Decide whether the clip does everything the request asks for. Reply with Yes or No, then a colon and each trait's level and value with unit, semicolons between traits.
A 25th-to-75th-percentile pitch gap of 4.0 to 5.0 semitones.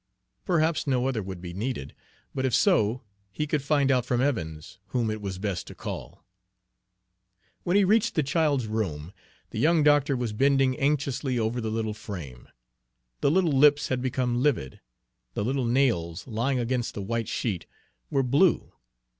Yes: average, 4.7 semitones